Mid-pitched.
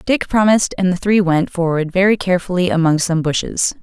Yes: medium, 180 Hz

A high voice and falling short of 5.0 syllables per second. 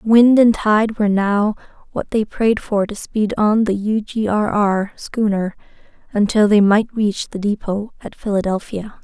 Yes: high, 210 Hz; 4.2 syllables/s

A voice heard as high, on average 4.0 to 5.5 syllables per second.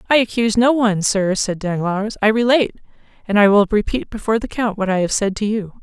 No: high, 210 Hz; 6.2 syllables/s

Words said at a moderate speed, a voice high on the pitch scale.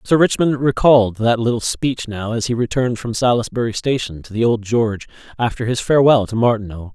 No: average, 190 wpm; low, 115 Hz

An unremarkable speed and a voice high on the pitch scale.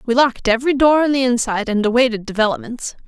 Yes: average, 195 wpm; high, 245 Hz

